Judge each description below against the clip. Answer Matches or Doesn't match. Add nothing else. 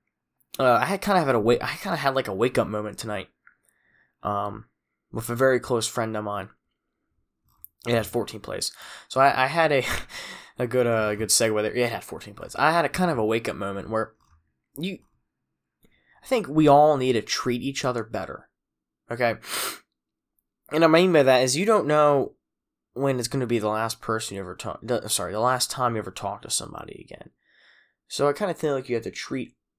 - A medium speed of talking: Doesn't match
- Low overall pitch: Matches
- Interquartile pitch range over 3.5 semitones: Matches